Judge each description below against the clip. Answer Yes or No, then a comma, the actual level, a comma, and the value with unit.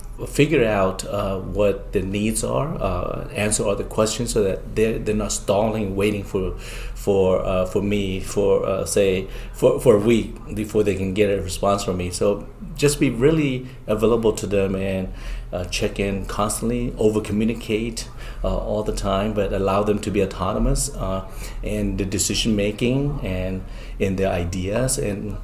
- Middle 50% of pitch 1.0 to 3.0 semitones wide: Yes, narrow, 2.4 semitones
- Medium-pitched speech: No, low, 105 Hz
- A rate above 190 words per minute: No, average, 170 wpm